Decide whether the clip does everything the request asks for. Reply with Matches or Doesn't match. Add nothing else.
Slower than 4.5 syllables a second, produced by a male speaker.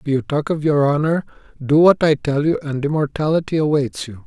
Doesn't match